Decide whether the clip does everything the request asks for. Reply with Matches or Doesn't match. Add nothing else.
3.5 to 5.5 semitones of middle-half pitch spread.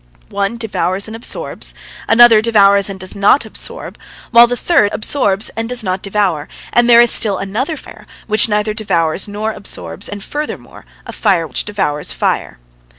Doesn't match